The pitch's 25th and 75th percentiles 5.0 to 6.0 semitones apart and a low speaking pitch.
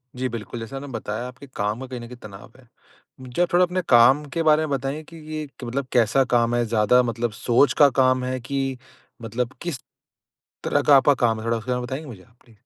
No: average, 2.9 semitones; low, 125 Hz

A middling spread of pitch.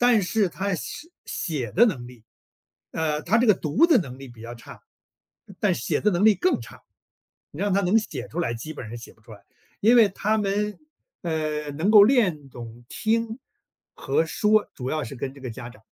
No: wide, 8.3 semitones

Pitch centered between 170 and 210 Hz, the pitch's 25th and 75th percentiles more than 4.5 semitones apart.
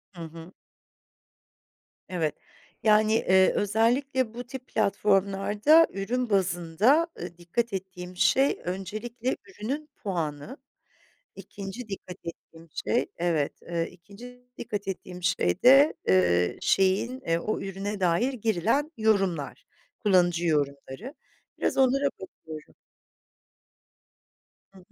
Yes: high, 195 Hz; wide, 5.4 semitones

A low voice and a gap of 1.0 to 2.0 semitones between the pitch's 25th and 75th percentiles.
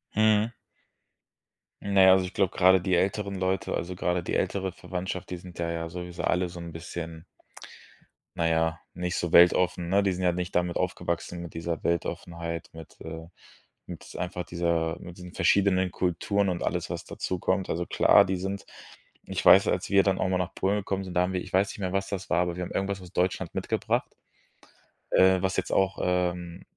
Yes: very low, 90 Hz; narrow, 1.7 semitones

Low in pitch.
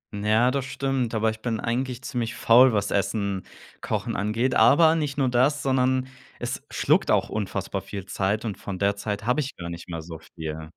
Yes: low, 110 Hz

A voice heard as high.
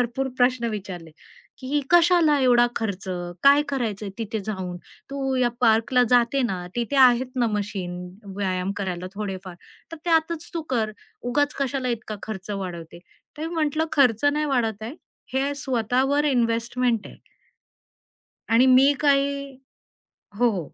Yes: high, 245 Hz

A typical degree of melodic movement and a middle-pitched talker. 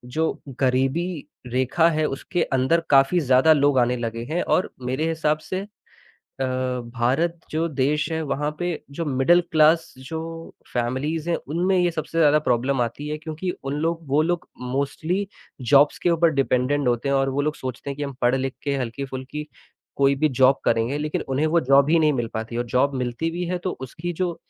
Yes: average, 3.8 semitones; medium, 145 Hz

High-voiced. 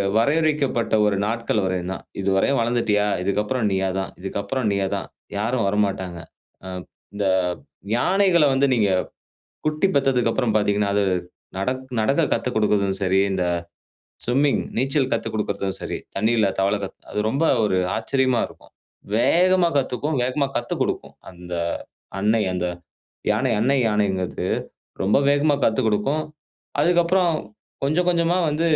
No: low, 115 Hz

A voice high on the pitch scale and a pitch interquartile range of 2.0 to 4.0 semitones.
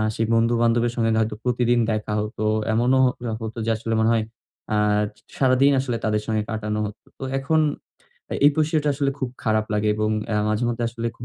No: low, 115 Hz; narrow, 2.6 semitones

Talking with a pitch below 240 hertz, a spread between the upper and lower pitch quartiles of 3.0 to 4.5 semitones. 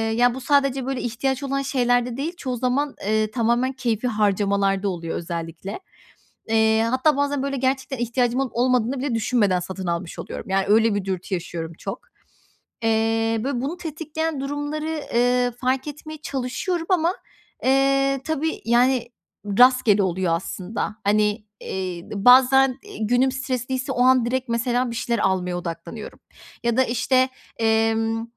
No: high, 245 Hz; average, 3.9 semitones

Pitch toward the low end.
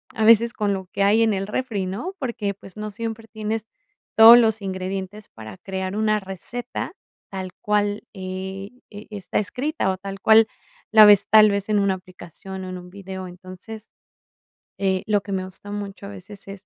No: high, 200 Hz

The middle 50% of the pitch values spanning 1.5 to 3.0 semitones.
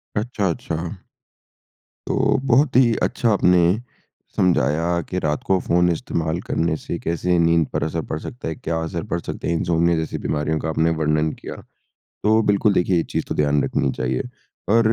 Yes: average, 2.7 semitones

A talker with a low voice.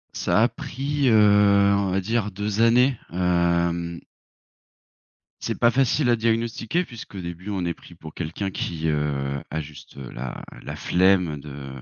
Yes: very low, 95 Hz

